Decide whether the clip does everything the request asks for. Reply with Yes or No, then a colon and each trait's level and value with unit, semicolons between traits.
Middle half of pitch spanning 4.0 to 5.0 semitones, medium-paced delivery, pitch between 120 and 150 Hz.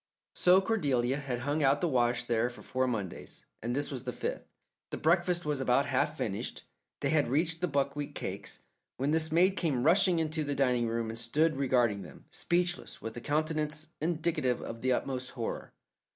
Yes: average, 4.6 semitones; average, 185 wpm; medium, 140 Hz